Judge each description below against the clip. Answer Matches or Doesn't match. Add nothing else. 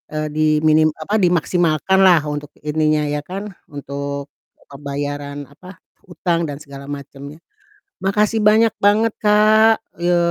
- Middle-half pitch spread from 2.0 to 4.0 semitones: Doesn't match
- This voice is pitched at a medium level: Matches